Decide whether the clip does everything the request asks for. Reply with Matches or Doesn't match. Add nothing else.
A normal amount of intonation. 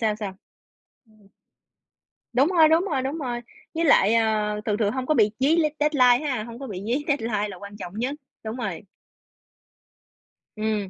Matches